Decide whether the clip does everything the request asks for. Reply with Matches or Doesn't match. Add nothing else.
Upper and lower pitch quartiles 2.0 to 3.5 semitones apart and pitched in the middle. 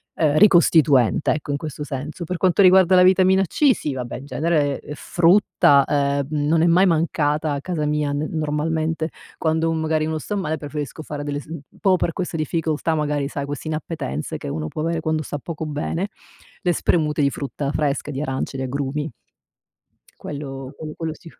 Matches